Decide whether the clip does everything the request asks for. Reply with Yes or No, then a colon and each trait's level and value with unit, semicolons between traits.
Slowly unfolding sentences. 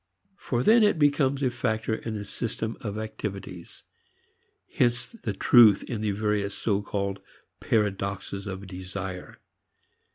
Yes: slow, 130 wpm